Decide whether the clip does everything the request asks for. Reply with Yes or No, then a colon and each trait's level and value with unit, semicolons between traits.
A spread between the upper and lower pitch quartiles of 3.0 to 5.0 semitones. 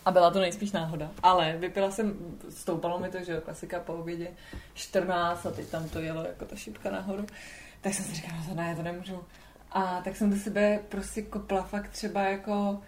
No: narrow, 2.6 semitones